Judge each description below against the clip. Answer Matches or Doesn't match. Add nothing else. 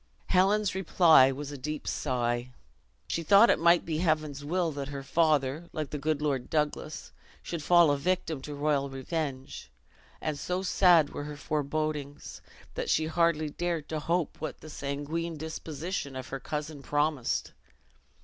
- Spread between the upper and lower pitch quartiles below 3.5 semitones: Matches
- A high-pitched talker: Doesn't match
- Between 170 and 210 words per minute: Doesn't match